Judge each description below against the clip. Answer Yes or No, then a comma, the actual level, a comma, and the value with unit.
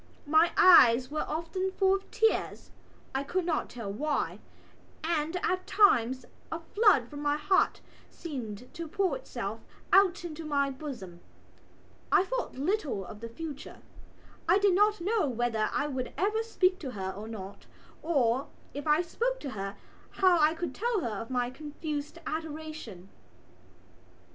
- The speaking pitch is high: Yes, very high, 305 Hz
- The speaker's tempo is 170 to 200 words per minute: No, average, 155 wpm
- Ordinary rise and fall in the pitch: No, wide, 6.6 semitones